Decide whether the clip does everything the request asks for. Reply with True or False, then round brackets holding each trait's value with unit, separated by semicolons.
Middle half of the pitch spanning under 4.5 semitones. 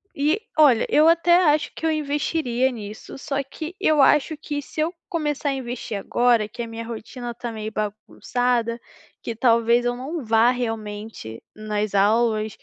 False (4.8 semitones)